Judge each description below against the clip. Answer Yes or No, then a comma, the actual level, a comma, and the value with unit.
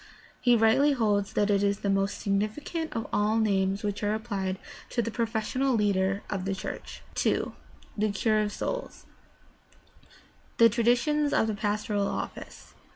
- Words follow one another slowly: No, average, 160 wpm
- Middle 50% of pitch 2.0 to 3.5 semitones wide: Yes, narrow, 2.5 semitones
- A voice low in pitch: No, high, 215 Hz